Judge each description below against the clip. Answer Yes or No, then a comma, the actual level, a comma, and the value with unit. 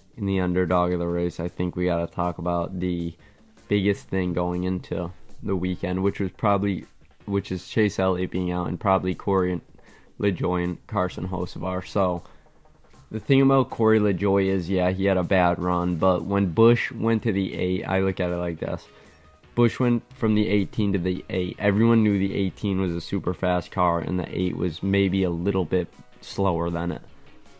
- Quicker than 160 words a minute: Yes, average, 195 wpm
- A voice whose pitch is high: No, very low, 90 Hz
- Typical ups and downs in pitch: No, narrow, 2.1 semitones